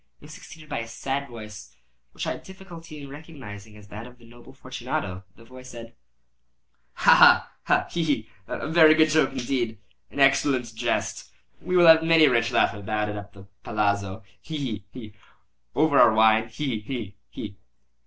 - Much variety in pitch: Yes, wide, 5.7 semitones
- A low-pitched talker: Yes, low, 120 Hz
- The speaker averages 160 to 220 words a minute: Yes, average, 165 wpm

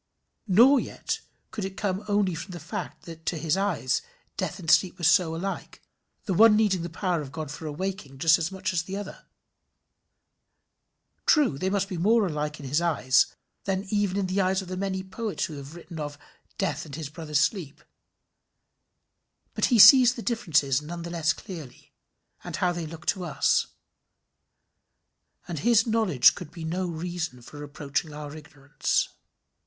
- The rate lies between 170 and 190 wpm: Yes, average, 175 wpm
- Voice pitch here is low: No, medium, 175 Hz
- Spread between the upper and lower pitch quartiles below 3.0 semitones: No, average, 4.1 semitones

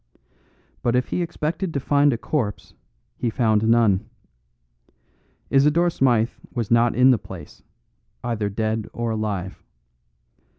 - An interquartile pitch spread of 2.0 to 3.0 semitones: No, average, 3.8 semitones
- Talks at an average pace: No, slow, 125 wpm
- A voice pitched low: Yes, low, 115 Hz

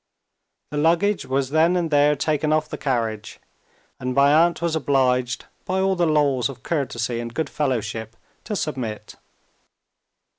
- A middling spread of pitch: Yes, average, 4.2 semitones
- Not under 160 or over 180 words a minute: No, average, 150 wpm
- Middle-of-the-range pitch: Yes, medium, 145 Hz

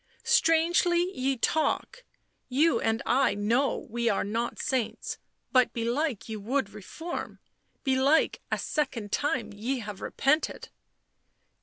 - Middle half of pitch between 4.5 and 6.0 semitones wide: Yes, wide, 5.5 semitones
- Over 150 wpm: No, average, 140 wpm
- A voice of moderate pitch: No, very high, 260 Hz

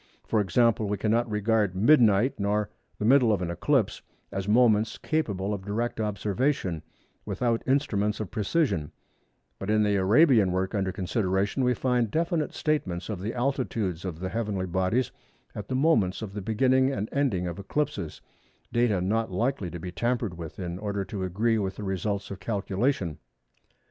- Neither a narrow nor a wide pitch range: Yes, average, 4.1 semitones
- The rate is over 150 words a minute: Yes, average, 165 wpm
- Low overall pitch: Yes, low, 105 Hz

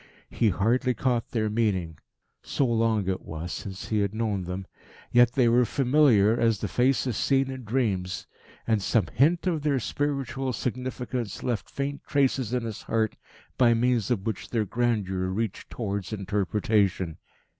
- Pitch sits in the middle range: No, low, 115 Hz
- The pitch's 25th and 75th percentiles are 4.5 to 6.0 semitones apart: No, average, 4.0 semitones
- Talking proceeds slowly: No, average, 155 wpm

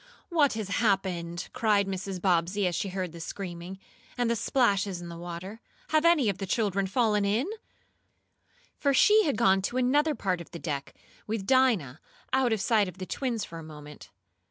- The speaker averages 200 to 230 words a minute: No, average, 185 wpm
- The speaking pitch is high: Yes, high, 200 Hz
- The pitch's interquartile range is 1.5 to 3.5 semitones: No, average, 5.2 semitones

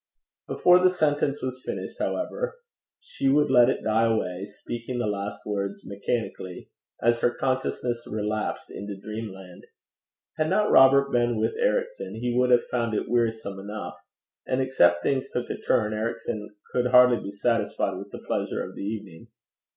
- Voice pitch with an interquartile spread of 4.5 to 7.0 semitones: No, average, 4.0 semitones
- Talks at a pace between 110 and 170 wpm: Yes, average, 160 wpm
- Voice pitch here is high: No, low, 115 Hz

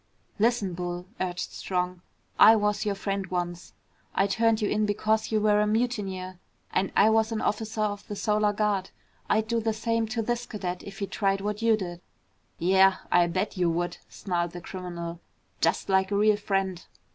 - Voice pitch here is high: Yes, high, 200 Hz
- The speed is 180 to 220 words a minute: Yes, average, 185 wpm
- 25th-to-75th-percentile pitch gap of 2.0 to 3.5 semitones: Yes, average, 2.8 semitones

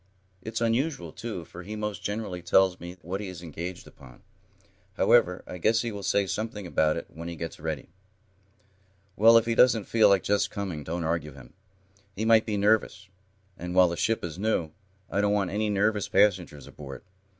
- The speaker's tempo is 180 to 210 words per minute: Yes, average, 190 wpm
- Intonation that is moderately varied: Yes, average, 4.0 semitones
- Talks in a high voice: No, very low, 95 Hz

